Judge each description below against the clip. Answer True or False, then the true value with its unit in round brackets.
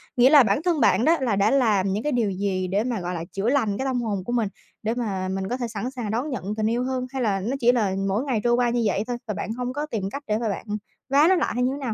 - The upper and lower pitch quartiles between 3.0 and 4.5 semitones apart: True (4.0 semitones)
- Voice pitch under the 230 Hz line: False (235 Hz)